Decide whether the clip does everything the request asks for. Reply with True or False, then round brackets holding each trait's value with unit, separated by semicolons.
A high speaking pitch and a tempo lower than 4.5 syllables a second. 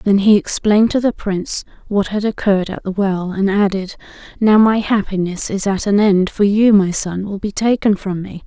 False (200 Hz; 5.0 syllables/s)